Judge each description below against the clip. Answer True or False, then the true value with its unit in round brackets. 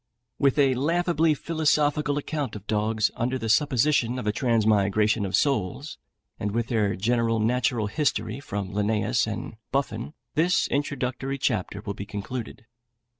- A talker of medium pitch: False (120 Hz)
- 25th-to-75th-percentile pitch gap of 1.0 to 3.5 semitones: False (4.9 semitones)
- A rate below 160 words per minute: True (140 wpm)